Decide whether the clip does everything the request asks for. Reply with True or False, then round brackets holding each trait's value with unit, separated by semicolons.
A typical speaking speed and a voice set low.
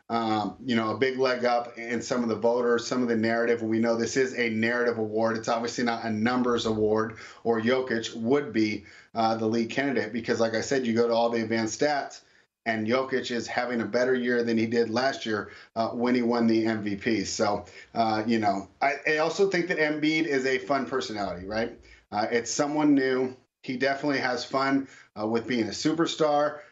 False (210 wpm; 120 Hz)